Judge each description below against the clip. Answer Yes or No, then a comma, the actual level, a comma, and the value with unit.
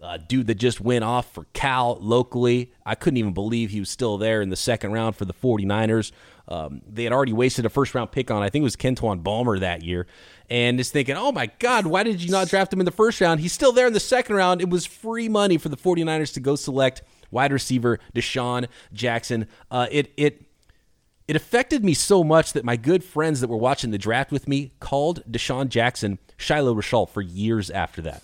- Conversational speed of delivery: No, fast, 225 wpm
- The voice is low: Yes, low, 125 Hz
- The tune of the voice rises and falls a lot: Yes, wide, 5.7 semitones